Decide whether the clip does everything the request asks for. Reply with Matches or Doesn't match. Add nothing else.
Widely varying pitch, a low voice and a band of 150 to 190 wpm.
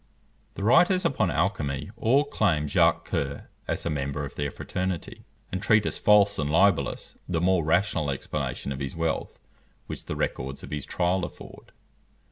Matches